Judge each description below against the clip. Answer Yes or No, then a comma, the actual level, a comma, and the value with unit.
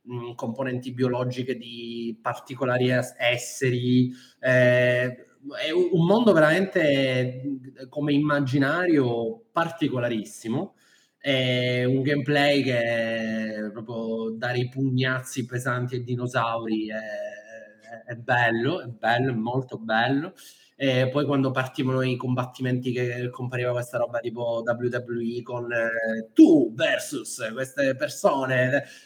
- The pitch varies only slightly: Yes, narrow, 2.3 semitones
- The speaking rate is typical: No, slow, 105 wpm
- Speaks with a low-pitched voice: Yes, low, 125 Hz